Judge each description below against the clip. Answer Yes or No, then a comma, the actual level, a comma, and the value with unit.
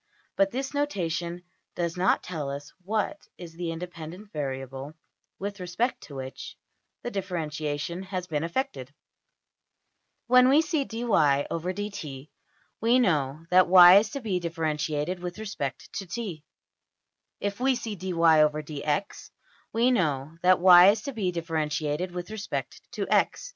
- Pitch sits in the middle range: Yes, medium, 180 Hz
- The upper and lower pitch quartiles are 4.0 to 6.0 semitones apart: Yes, average, 5.1 semitones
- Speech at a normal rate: No, slow, 130 wpm